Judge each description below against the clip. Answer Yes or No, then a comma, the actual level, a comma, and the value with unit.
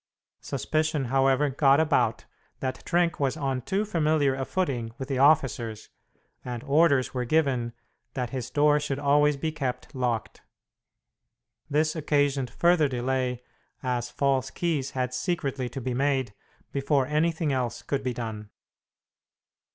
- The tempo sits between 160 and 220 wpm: No, slow, 135 wpm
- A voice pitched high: No, low, 135 Hz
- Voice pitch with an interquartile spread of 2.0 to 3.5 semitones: Yes, average, 2.9 semitones